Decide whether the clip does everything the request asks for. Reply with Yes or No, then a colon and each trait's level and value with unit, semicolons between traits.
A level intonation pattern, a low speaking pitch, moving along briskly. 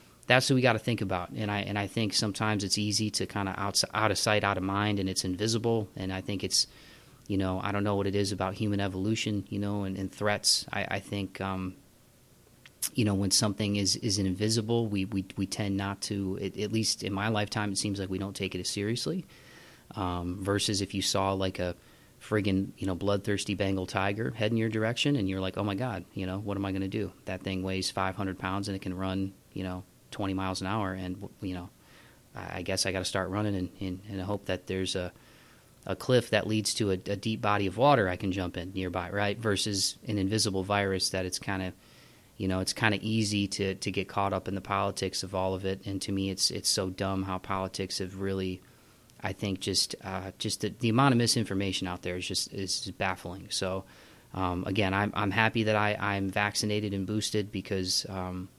Yes: narrow, 1.8 semitones; low, 100 Hz; fast, 235 wpm